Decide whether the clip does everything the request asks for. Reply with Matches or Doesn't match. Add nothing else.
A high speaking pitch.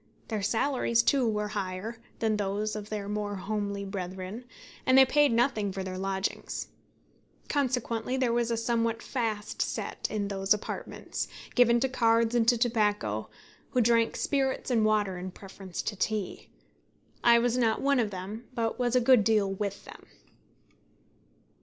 Matches